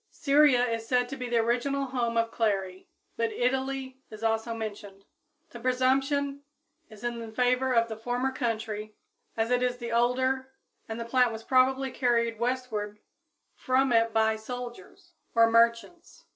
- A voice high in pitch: Yes, high, 240 Hz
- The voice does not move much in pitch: Yes, narrow, 2.3 semitones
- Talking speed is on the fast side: No, average, 155 wpm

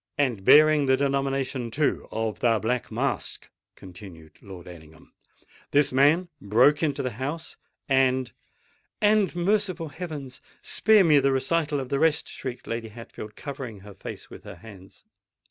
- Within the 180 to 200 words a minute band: No, slow, 135 wpm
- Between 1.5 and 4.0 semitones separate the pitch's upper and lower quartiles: No, average, 5.1 semitones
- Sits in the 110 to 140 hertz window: Yes, low, 135 Hz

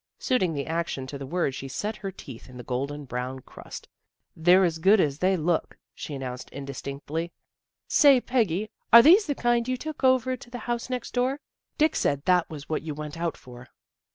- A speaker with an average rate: No, fast, 210 wpm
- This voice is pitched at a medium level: Yes, medium, 170 Hz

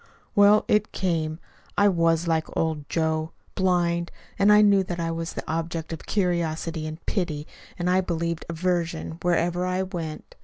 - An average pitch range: No, narrow, 2.1 semitones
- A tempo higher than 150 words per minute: Yes, average, 160 wpm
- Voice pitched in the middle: Yes, medium, 170 Hz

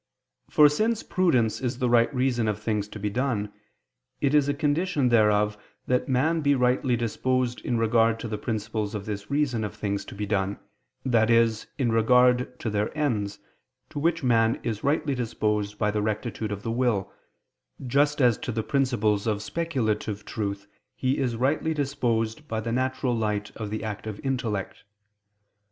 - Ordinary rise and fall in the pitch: Yes, average, 3.7 semitones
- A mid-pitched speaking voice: No, low, 115 Hz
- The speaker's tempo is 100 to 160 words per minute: No, average, 175 wpm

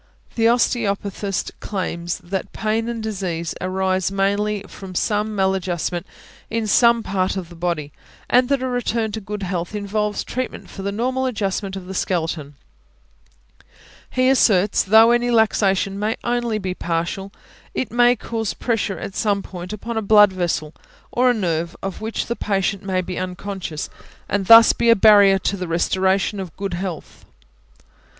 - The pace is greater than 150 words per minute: Yes, average, 160 wpm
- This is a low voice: No, high, 200 Hz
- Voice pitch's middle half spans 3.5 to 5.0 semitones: No, average, 3.1 semitones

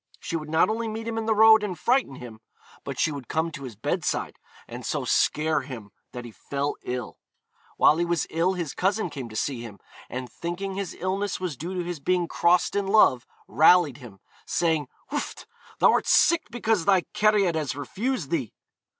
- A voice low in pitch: No, medium, 170 Hz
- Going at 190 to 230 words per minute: Yes, average, 195 wpm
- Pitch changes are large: Yes, wide, 6.1 semitones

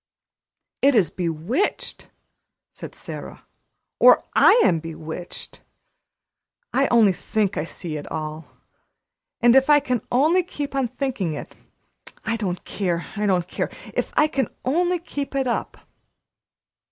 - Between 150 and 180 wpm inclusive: No, slow, 135 wpm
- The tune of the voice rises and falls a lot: Yes, wide, 7.9 semitones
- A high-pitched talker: Yes, high, 230 Hz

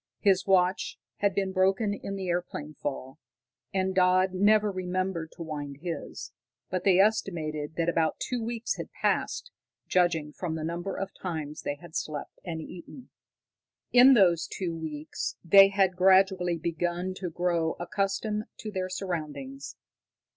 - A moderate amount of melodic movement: Yes, average, 3.2 semitones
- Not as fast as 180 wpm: Yes, average, 145 wpm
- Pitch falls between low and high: Yes, medium, 180 Hz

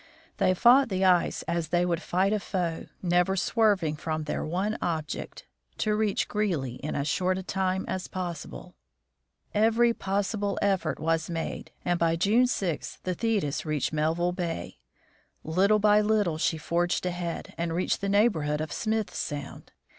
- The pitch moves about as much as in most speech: Yes, average, 3.8 semitones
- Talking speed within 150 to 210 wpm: Yes, average, 160 wpm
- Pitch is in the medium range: Yes, medium, 180 Hz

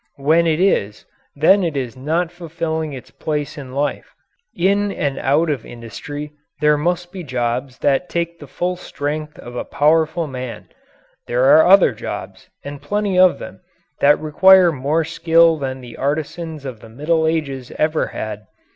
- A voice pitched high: No, medium, 150 Hz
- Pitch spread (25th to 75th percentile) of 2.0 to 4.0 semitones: Yes, average, 3.7 semitones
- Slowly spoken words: No, average, 165 wpm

